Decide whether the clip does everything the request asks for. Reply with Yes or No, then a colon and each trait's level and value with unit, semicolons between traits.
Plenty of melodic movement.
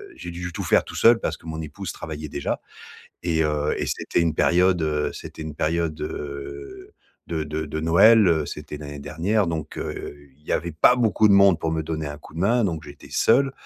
No: average, 3.5 semitones